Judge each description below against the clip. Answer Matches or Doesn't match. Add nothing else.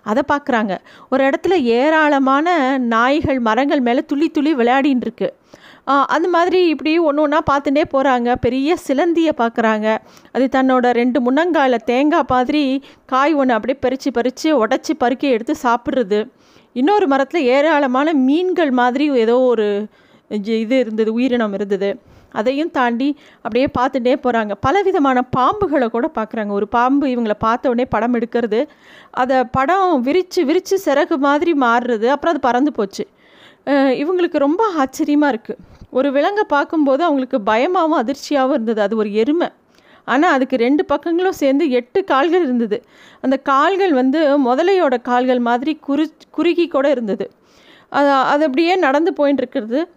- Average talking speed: Doesn't match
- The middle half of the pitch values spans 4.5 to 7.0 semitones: Doesn't match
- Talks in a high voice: Matches